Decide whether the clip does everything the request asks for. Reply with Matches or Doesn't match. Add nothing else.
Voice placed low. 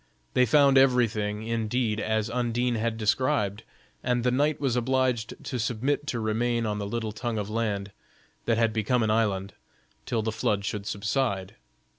Matches